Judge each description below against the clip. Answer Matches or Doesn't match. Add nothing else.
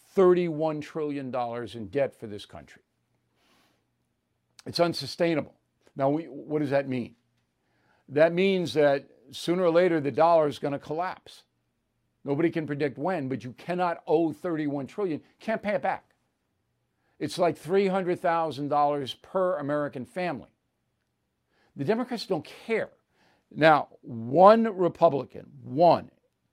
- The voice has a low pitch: Doesn't match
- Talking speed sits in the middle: Doesn't match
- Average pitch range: Matches